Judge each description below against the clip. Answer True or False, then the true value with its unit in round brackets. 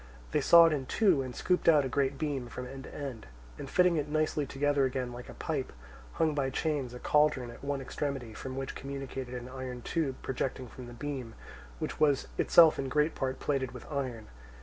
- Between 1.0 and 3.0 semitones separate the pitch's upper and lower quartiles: True (2.7 semitones)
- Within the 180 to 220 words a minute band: True (205 wpm)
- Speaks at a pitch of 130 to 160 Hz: True (135 Hz)